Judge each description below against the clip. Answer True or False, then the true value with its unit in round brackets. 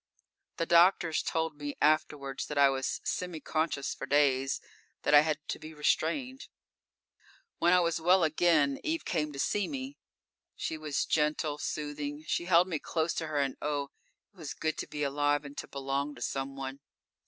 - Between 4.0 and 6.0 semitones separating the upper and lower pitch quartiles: False (2.7 semitones)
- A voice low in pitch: False (150 Hz)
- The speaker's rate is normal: True (180 wpm)